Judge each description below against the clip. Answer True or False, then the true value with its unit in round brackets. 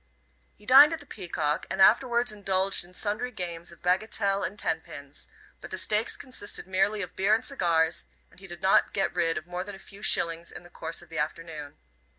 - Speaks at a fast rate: True (210 wpm)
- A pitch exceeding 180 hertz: True (190 Hz)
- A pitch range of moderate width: True (3.6 semitones)